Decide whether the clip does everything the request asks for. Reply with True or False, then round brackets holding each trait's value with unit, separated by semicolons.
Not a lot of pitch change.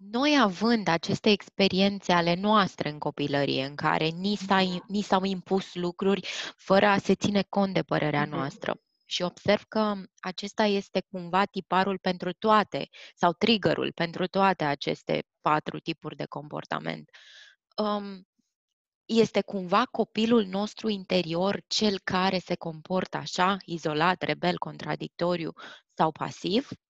False (3.0 semitones)